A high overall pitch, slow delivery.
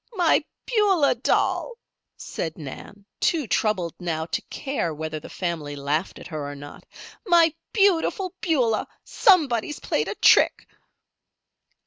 Yes: high, 215 Hz; slow, 125 wpm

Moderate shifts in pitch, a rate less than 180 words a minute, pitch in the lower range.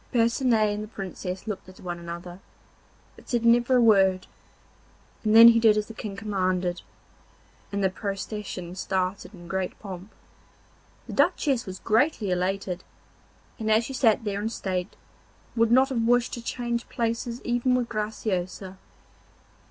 No: average, 3.7 semitones; average, 150 wpm; high, 210 Hz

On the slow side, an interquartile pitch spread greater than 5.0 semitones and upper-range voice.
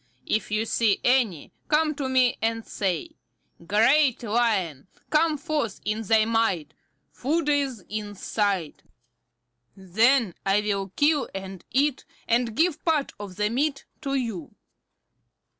Yes: slow, 130 wpm; wide, 5.4 semitones; high, 230 Hz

